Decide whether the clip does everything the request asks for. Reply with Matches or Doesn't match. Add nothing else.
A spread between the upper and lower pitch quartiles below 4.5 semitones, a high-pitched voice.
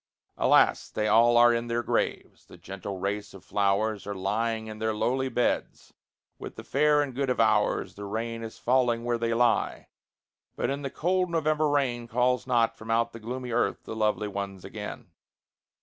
Doesn't match